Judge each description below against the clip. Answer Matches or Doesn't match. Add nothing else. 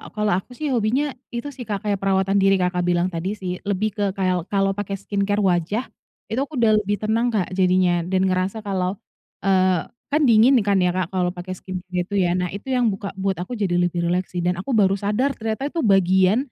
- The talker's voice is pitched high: Matches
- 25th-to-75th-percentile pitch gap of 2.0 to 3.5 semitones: Matches